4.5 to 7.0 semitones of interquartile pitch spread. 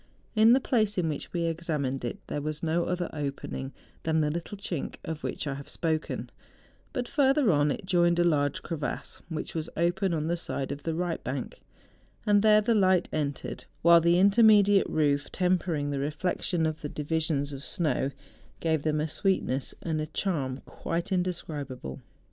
No: average, 3.8 semitones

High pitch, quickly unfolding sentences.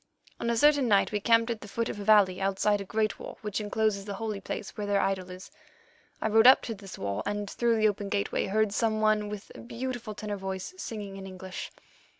Yes: high, 210 Hz; fast, 230 wpm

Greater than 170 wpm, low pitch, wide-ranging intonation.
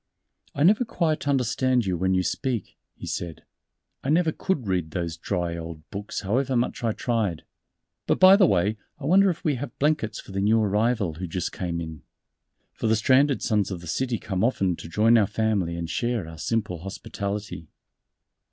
Yes: average, 190 wpm; low, 105 Hz; wide, 6.3 semitones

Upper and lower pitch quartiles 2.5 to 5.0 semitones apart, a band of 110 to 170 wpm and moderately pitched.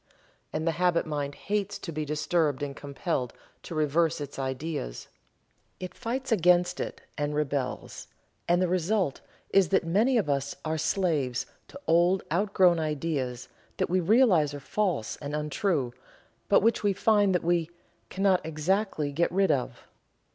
Yes: average, 4.6 semitones; average, 155 wpm; medium, 165 Hz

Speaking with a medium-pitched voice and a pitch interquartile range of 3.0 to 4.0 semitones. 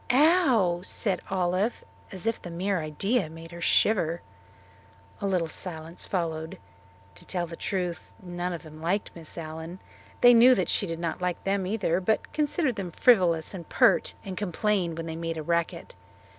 Yes: medium, 180 Hz; average, 3.3 semitones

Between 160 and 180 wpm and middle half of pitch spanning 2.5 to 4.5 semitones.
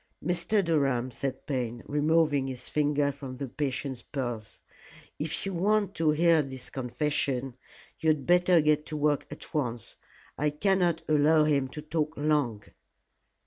No: average, 145 wpm; average, 3.2 semitones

